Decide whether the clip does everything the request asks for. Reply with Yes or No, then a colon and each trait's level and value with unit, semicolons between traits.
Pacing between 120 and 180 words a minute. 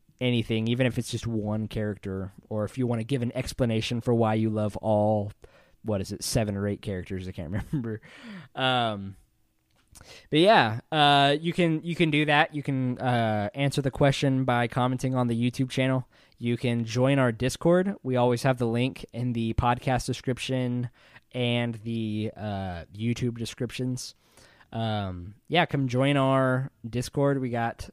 Yes: average, 170 wpm